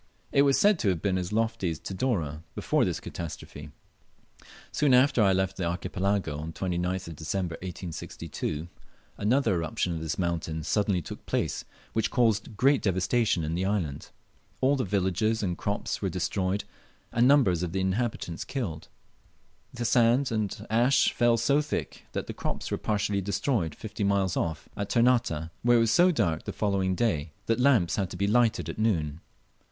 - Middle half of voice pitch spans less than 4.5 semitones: No, average, 5.2 semitones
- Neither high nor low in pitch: No, low, 100 Hz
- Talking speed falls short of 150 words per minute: No, average, 175 wpm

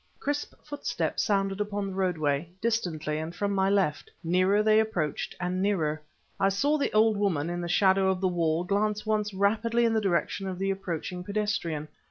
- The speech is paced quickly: No, average, 185 wpm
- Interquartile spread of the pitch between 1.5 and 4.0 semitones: Yes, average, 3.2 semitones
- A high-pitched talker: Yes, high, 195 Hz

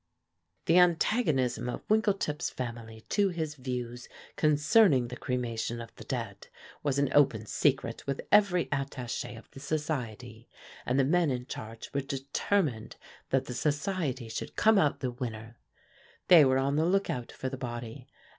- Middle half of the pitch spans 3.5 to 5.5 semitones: Yes, average, 4.3 semitones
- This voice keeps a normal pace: Yes, average, 155 wpm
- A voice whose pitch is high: No, low, 135 Hz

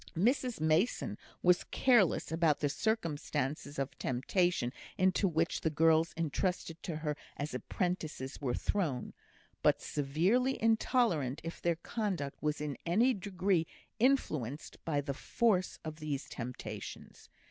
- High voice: No, medium, 165 Hz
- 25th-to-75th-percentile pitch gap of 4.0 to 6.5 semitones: Yes, average, 4.9 semitones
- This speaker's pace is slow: Yes, slow, 125 wpm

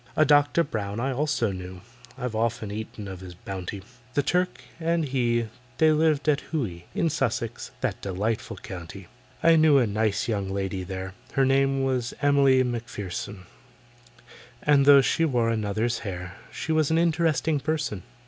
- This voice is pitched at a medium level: No, low, 120 Hz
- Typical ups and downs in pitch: No, wide, 6.4 semitones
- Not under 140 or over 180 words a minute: Yes, average, 160 wpm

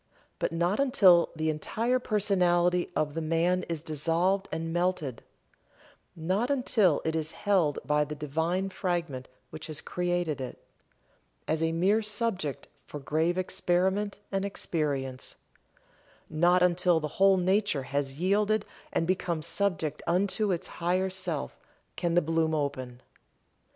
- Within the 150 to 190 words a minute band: No, slow, 135 wpm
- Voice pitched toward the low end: No, medium, 175 Hz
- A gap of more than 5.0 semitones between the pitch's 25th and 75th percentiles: No, average, 3.5 semitones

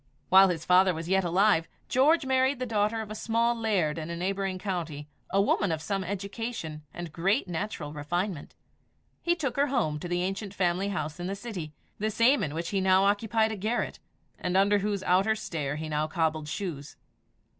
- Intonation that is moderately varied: Yes, average, 4.5 semitones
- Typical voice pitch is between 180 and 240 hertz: Yes, high, 190 Hz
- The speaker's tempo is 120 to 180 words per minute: No, average, 195 wpm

